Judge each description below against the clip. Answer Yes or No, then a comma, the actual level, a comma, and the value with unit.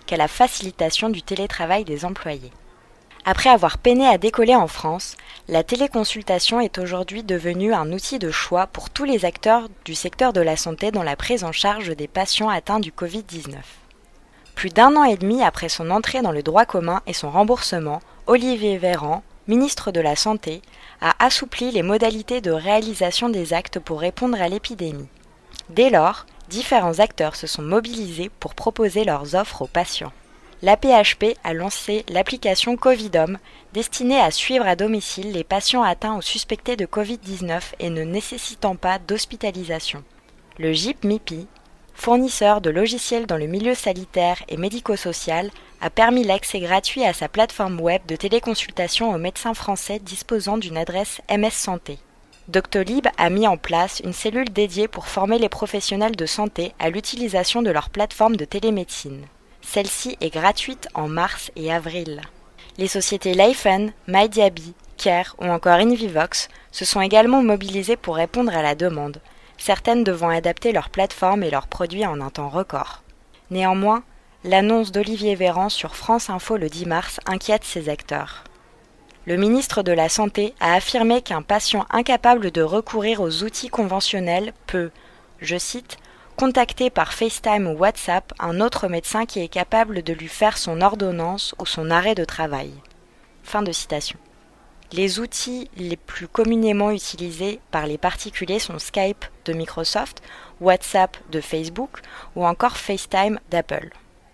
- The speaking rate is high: No, average, 155 wpm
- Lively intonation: No, average, 4.4 semitones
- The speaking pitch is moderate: No, high, 195 Hz